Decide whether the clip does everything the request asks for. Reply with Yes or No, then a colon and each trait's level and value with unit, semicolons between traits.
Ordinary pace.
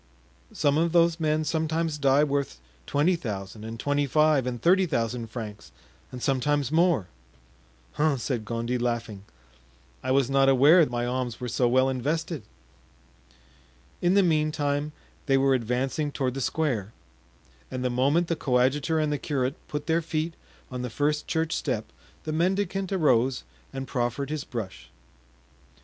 Yes: average, 150 wpm